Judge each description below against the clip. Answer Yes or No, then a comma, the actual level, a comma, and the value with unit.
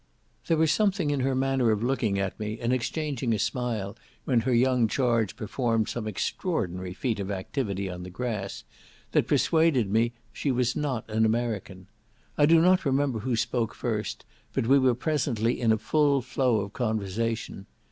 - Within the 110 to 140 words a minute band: No, average, 175 wpm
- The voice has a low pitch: Yes, low, 120 Hz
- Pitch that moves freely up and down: No, average, 3.8 semitones